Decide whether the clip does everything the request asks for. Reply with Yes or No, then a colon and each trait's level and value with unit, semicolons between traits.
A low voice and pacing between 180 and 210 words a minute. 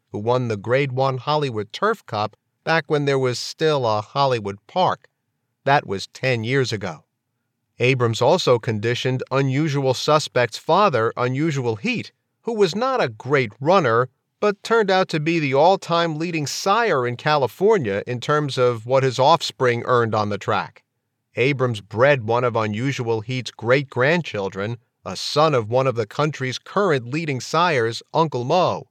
No: low, 130 Hz; average, 160 wpm